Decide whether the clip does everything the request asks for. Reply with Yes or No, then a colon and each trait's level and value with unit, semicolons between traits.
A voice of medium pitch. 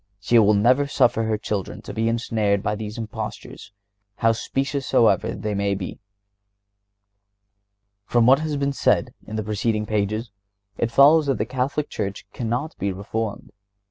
No: low, 110 Hz